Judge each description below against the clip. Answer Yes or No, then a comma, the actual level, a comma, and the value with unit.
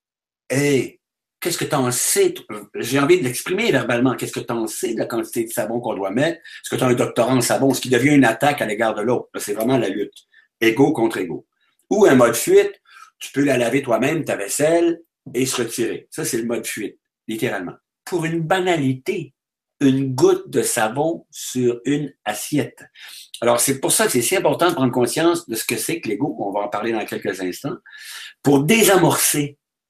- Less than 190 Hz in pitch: Yes, low, 135 Hz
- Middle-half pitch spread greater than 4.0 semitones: Yes, wide, 5.5 semitones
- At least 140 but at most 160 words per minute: No, average, 210 wpm